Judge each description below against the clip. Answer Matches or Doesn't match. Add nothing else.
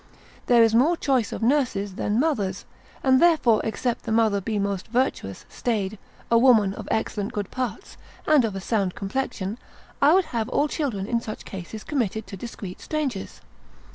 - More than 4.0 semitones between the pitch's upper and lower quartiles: Matches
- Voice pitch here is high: Matches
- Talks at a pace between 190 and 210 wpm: Doesn't match